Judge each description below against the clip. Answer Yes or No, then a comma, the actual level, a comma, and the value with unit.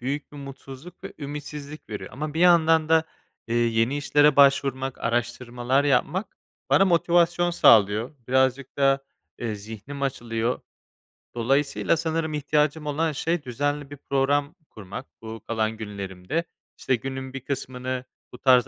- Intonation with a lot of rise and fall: No, average, 3.6 semitones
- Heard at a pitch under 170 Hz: Yes, low, 135 Hz